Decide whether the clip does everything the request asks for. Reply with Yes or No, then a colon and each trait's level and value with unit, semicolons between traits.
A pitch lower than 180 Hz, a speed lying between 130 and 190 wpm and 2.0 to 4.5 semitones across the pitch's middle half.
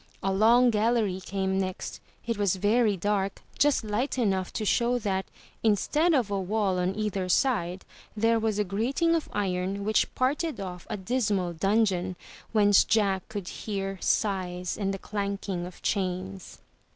No: high, 200 Hz; average, 155 wpm; average, 2.8 semitones